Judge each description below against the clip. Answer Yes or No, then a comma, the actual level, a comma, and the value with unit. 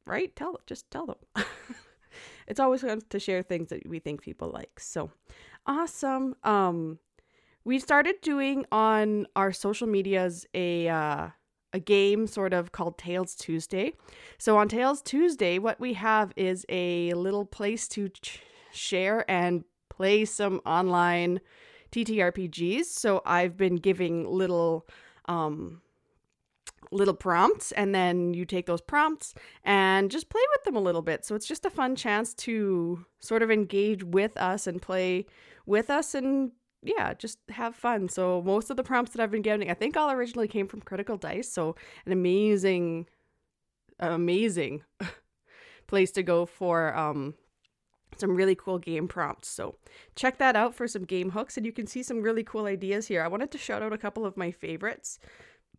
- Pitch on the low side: No, high, 200 Hz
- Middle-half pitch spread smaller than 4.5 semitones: No, average, 5.0 semitones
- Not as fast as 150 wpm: No, average, 170 wpm